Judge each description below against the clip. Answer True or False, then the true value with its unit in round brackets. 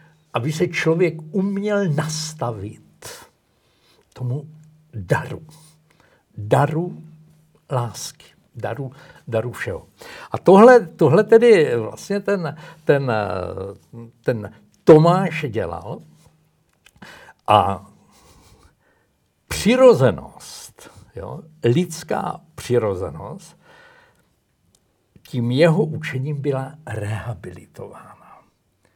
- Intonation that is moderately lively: False (5.7 semitones)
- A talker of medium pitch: True (150 Hz)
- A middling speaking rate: False (65 wpm)